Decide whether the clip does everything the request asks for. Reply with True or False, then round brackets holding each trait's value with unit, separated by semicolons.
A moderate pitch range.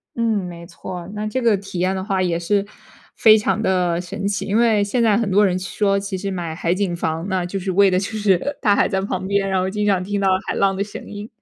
False (2.0 semitones)